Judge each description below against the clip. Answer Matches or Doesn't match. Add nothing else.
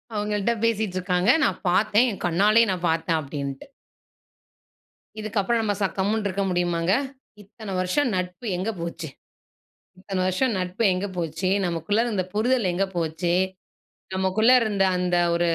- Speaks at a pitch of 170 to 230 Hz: Matches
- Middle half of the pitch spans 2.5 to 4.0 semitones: Matches